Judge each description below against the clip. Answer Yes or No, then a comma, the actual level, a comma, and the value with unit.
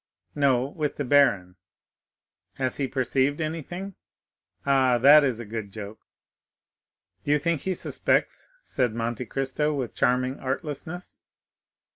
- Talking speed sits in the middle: No, slow, 125 wpm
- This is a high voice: No, low, 135 Hz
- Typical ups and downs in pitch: Yes, average, 3.3 semitones